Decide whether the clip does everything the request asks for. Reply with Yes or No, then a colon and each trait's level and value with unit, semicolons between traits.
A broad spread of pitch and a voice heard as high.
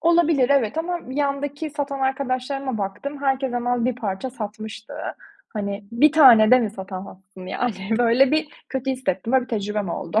No: average, 4.7 semitones; very high, 250 Hz